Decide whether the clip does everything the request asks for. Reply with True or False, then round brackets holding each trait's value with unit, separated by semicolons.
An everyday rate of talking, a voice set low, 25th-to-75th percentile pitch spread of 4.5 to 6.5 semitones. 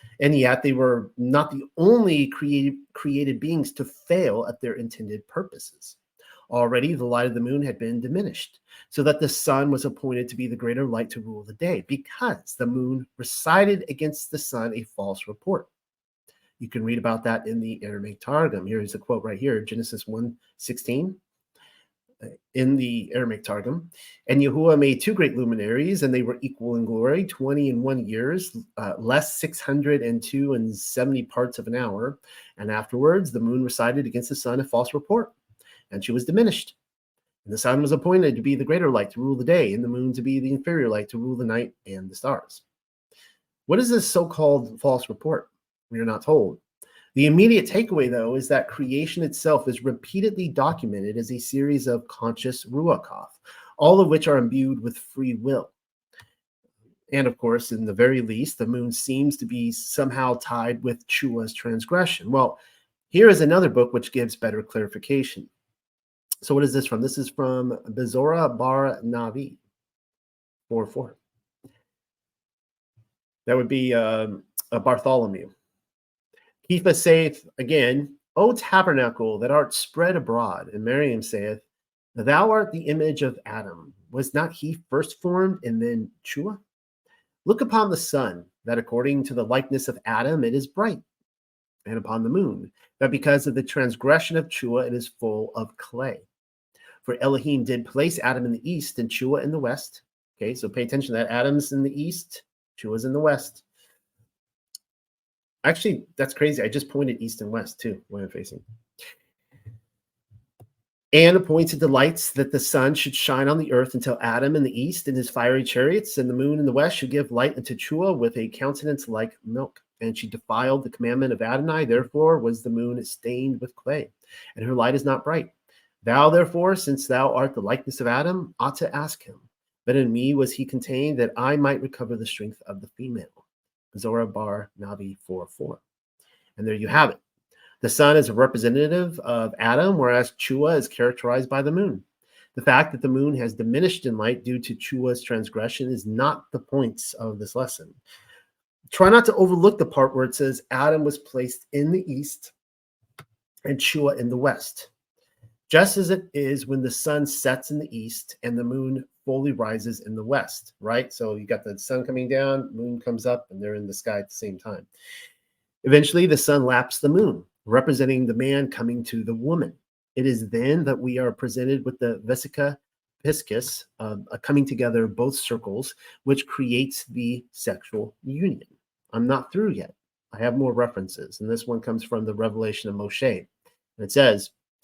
False (180 wpm; 130 Hz; 3.7 semitones)